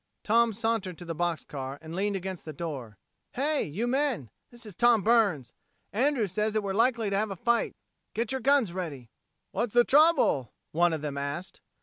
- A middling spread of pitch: No, wide, 6.3 semitones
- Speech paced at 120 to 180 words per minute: No, average, 195 wpm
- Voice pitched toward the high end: Yes, high, 200 Hz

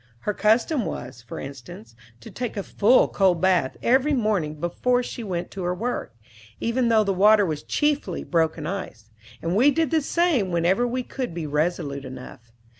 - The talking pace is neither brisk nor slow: Yes, average, 180 wpm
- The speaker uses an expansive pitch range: Yes, wide, 7.4 semitones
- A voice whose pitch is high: Yes, high, 195 Hz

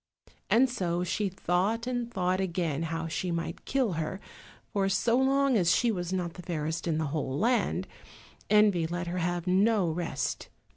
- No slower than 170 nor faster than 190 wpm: Yes, average, 175 wpm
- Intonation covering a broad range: No, average, 4.2 semitones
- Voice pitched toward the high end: No, medium, 180 Hz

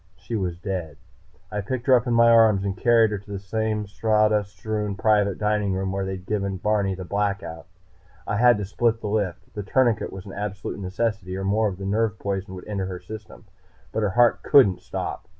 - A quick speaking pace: Yes, fast, 210 wpm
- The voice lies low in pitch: Yes, low, 105 Hz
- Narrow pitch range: Yes, narrow, 2.2 semitones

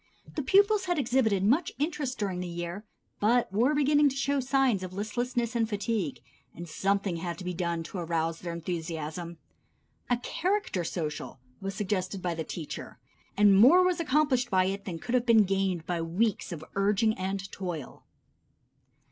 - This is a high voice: Yes, high, 200 Hz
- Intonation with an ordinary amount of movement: No, wide, 6.3 semitones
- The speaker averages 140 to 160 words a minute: No, average, 170 wpm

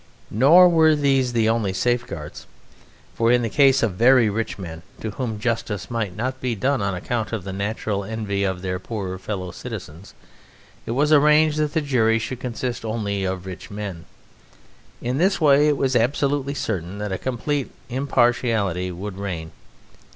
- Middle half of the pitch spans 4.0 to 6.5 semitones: Yes, average, 5.1 semitones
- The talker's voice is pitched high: No, low, 115 Hz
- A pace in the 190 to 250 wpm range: No, average, 170 wpm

